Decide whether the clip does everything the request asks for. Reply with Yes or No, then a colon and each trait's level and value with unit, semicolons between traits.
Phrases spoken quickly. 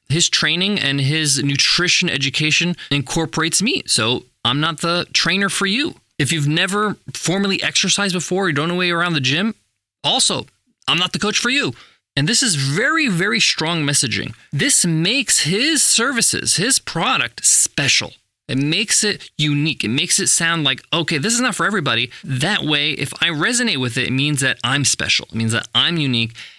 No: average, 185 wpm